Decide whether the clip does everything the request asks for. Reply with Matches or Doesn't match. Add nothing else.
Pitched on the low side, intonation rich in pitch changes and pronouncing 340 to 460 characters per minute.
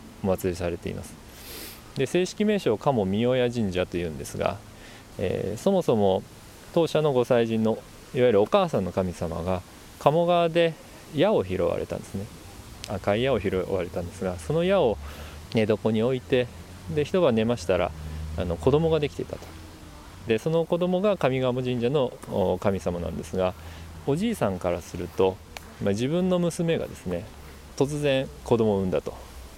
Doesn't match